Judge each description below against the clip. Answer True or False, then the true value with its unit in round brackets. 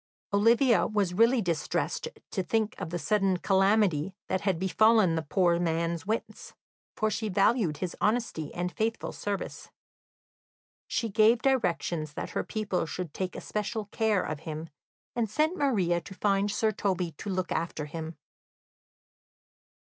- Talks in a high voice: True (195 Hz)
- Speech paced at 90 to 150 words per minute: True (145 wpm)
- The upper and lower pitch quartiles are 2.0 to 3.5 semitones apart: False (4.1 semitones)